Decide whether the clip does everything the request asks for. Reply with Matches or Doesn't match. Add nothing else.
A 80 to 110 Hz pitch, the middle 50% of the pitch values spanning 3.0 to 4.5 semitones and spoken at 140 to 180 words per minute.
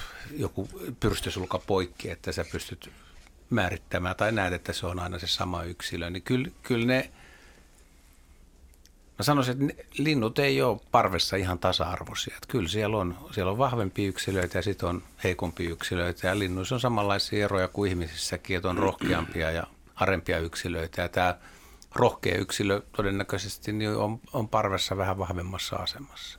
Matches